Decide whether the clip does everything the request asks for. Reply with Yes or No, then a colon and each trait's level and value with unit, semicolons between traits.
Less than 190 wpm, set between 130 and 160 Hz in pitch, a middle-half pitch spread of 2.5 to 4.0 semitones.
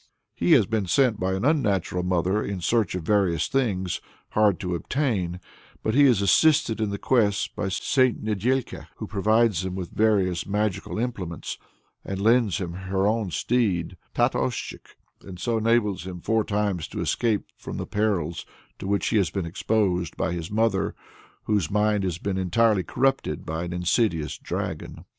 No: average, 170 wpm; low, 100 Hz; average, 3.6 semitones